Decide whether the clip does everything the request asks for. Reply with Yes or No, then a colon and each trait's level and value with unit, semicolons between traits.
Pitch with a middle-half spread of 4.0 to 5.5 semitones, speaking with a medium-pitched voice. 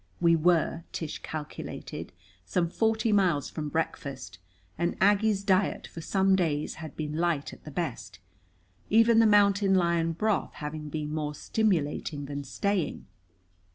Yes: average, 4.8 semitones; medium, 170 Hz